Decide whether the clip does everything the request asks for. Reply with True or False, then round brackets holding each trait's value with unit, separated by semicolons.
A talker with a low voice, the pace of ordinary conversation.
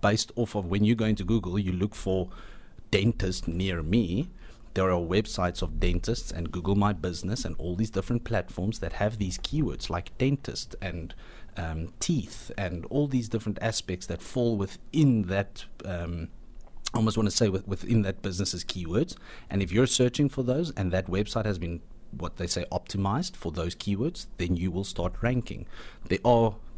True (100 Hz; 180 wpm)